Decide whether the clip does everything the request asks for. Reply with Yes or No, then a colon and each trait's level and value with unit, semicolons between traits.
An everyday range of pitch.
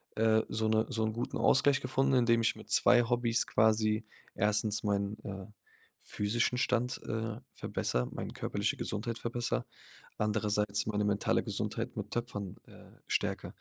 No: narrow, 2.2 semitones